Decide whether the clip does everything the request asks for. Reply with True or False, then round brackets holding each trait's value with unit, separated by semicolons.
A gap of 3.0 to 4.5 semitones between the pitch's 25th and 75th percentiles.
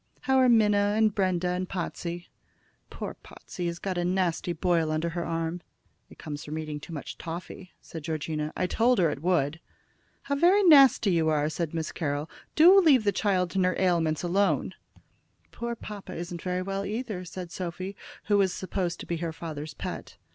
True (3.5 semitones)